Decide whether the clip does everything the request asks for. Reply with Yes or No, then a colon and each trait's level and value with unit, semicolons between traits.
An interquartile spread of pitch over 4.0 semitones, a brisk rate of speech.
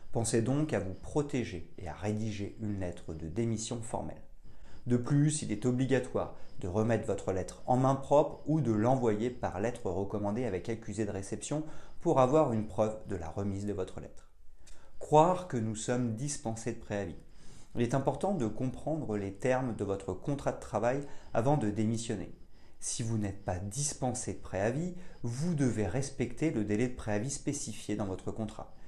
No: average, 4.5 semitones; average, 175 wpm